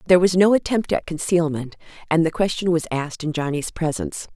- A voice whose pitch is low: No, medium, 170 Hz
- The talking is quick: No, average, 195 wpm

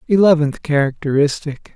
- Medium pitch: Yes, medium, 150 Hz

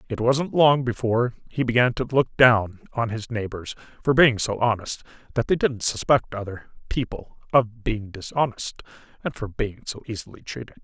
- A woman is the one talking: No, male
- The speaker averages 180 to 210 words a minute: No, average, 170 wpm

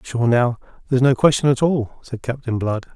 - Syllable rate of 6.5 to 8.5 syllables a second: No, 5.4 syllables/s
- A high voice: No, low, 125 Hz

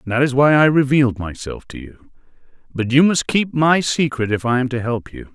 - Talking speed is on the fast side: Yes, fast, 225 wpm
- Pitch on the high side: No, low, 135 Hz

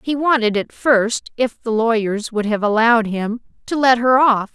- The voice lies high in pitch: Yes, high, 230 Hz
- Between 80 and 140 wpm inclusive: No, average, 200 wpm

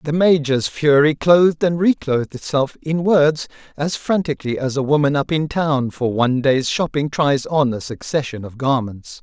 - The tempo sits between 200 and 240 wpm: No, average, 175 wpm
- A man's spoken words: Yes, male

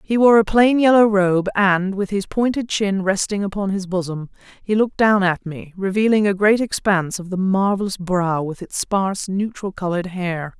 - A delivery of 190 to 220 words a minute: Yes, average, 195 wpm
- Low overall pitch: No, high, 195 Hz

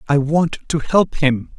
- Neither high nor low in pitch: Yes, medium, 150 Hz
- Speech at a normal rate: Yes, average, 190 wpm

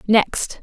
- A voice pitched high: Yes, high, 215 Hz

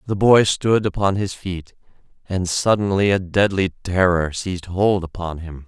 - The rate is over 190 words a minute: No, average, 150 wpm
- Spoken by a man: Yes, male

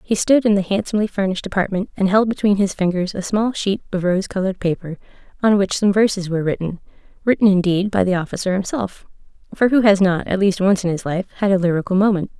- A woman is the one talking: Yes, female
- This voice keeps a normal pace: No, fast, 215 wpm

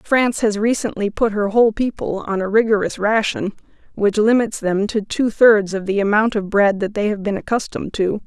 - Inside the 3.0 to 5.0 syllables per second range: No, 5.3 syllables/s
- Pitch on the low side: No, high, 210 Hz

